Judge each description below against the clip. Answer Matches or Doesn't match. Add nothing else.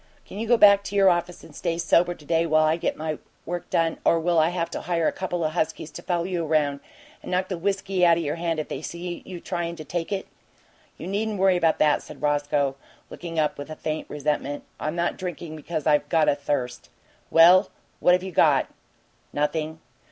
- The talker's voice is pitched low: Doesn't match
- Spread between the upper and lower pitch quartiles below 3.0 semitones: Matches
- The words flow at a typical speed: Doesn't match